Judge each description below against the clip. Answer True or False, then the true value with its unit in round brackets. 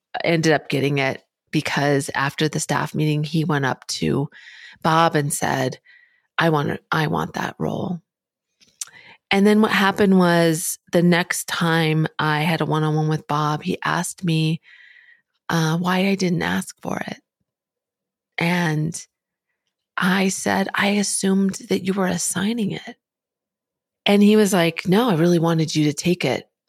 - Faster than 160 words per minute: False (155 wpm)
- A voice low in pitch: False (170 Hz)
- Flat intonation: False (3.8 semitones)